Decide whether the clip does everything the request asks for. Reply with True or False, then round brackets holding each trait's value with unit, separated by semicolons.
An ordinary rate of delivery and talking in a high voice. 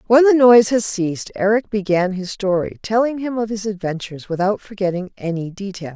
True (180 wpm; 200 Hz)